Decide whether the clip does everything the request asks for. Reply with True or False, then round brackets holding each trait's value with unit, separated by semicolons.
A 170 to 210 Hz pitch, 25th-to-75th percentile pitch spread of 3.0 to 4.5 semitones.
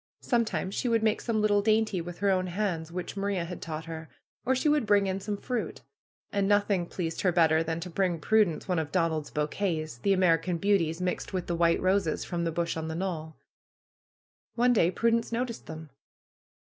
True (185 Hz; 3.9 semitones)